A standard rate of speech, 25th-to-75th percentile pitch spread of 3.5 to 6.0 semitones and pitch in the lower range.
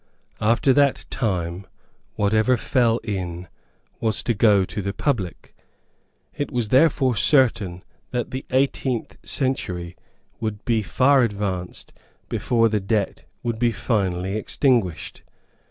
No: slow, 120 wpm; average, 4.6 semitones; low, 110 Hz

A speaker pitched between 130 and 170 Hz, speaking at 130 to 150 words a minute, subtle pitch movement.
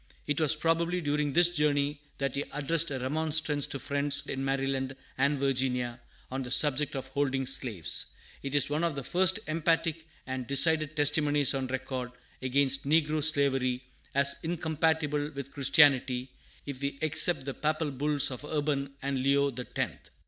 No: medium, 140 Hz; average, 160 wpm; narrow, 2.3 semitones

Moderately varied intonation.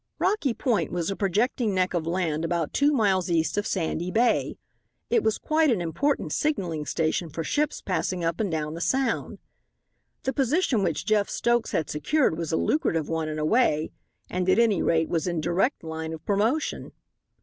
No: wide, 6.6 semitones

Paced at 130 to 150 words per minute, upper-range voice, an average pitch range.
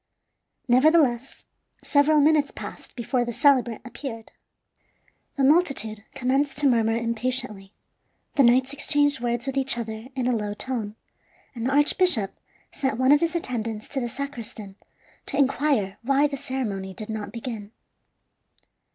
Yes: average, 140 wpm; very high, 255 Hz; average, 3.7 semitones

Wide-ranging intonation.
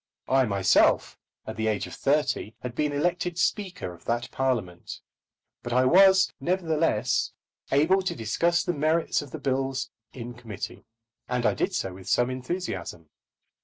Yes: wide, 6.5 semitones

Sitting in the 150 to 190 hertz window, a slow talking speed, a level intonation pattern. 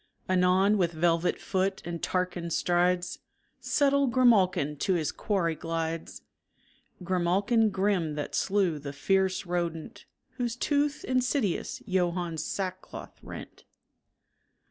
No: medium, 185 Hz; slow, 105 wpm; average, 3.3 semitones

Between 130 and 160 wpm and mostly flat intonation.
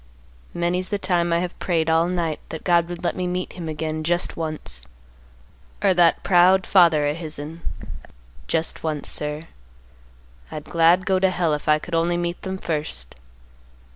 No: average, 170 wpm; narrow, 2.2 semitones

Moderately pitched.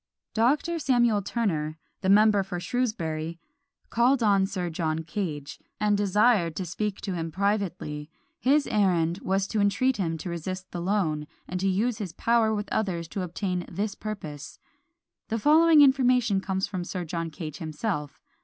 No: high, 195 Hz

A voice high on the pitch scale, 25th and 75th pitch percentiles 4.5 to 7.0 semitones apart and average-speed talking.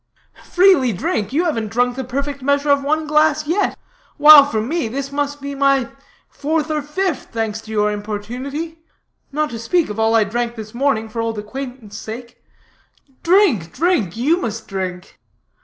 Yes: very high, 265 Hz; average, 5.2 semitones; average, 170 wpm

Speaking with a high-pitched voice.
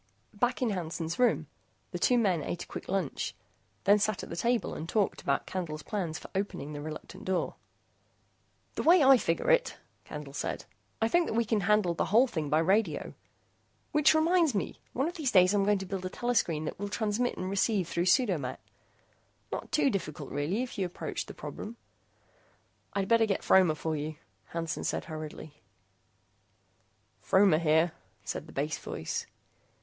Yes: high, 195 Hz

